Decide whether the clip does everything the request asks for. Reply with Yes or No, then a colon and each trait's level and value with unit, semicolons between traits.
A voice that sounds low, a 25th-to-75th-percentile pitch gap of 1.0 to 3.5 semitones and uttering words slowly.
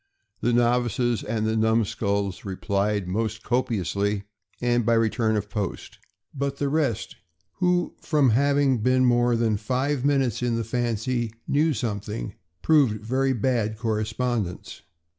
Yes: low, 115 Hz; average, 3.2 semitones; slow, 130 wpm